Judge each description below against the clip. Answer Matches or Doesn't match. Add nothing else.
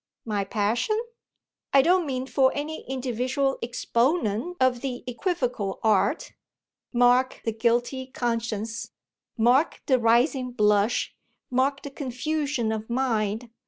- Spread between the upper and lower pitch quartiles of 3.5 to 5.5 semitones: Doesn't match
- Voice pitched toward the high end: Matches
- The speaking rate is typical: Doesn't match